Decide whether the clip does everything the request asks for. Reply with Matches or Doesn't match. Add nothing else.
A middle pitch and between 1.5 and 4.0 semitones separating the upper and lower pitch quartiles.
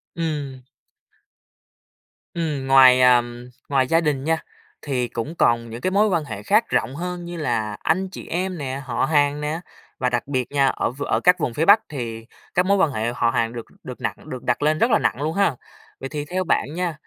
Doesn't match